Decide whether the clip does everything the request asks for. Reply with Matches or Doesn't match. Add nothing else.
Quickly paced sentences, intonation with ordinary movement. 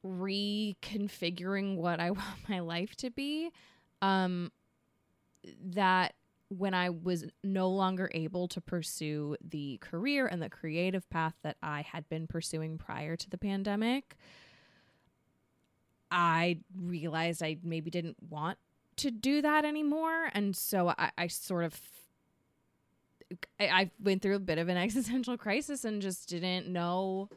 Doesn't match